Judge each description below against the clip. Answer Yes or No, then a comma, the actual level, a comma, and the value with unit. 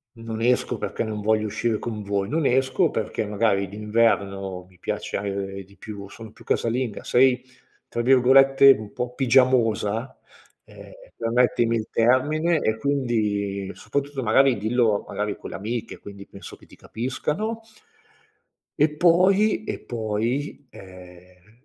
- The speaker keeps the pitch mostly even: No, average, 4.3 semitones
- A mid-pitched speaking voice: No, low, 115 Hz